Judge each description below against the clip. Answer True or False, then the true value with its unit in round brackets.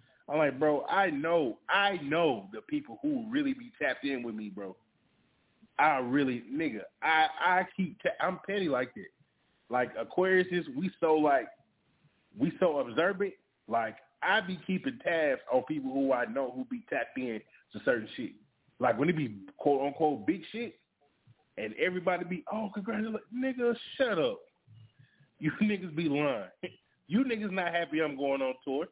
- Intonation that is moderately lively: False (8.0 semitones)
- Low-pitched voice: False (175 Hz)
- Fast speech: False (170 wpm)